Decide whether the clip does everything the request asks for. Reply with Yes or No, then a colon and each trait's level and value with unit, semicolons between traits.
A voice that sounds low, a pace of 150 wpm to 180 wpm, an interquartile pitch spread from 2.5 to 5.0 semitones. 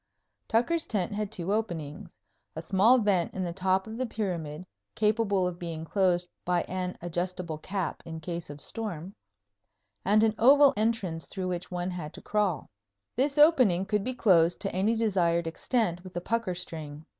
No: medium, 185 Hz; average, 170 wpm; average, 4.0 semitones